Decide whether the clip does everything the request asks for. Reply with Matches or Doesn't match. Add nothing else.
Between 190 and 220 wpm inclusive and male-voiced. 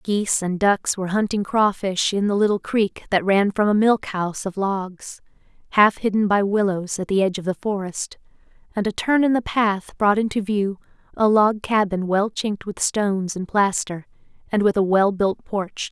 Doesn't match